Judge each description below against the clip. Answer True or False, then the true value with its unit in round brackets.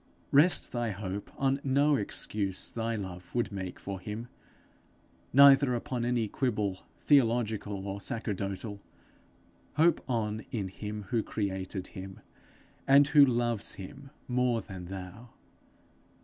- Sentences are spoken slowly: True (120 wpm)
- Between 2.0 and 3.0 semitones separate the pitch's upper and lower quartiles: False (4.2 semitones)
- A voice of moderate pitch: False (110 Hz)